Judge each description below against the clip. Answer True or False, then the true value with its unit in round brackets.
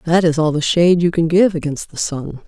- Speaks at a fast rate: True (265 wpm)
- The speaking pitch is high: False (165 Hz)